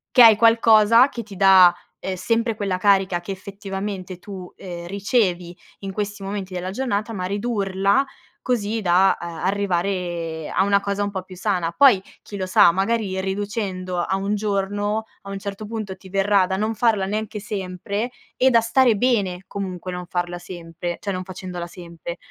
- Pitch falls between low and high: No, high, 195 Hz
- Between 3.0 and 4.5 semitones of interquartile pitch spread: No, narrow, 2.4 semitones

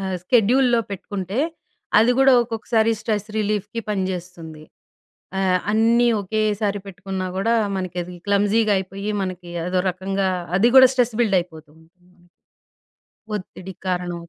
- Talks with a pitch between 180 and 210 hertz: Yes, high, 195 Hz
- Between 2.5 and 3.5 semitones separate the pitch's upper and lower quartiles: Yes, average, 3.2 semitones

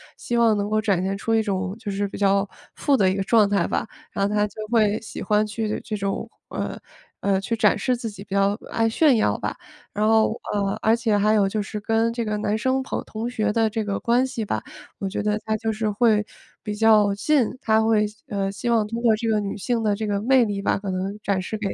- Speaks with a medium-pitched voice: No, high, 215 Hz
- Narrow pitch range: Yes, narrow, 2.0 semitones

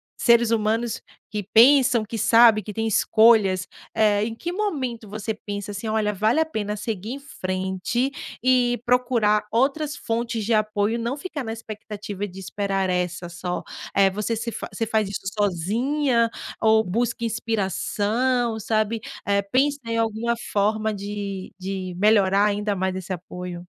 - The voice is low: No, high, 215 Hz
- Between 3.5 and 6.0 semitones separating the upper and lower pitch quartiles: No, average, 2.7 semitones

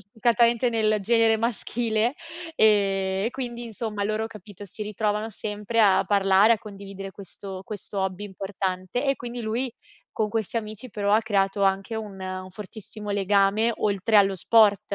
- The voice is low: No, high, 210 Hz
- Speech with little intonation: Yes, narrow, 2.3 semitones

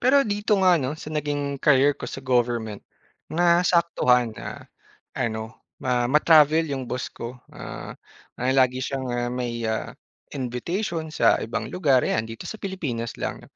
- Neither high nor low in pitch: No, low, 130 Hz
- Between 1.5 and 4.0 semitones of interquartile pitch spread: No, average, 5.1 semitones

